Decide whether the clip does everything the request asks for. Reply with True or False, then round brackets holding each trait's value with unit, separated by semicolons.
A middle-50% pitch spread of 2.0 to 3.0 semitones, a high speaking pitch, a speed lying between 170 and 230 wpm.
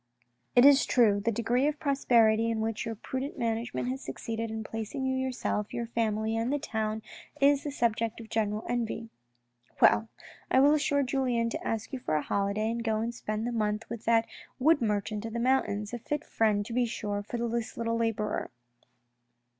True (2.5 semitones; 230 Hz; 195 wpm)